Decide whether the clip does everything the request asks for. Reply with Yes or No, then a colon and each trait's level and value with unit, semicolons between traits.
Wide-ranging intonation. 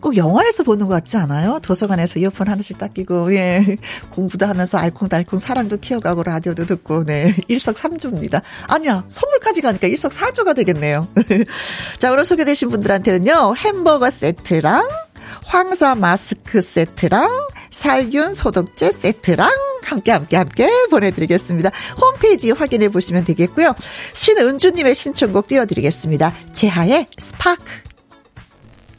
Yes: wide, 7.5 semitones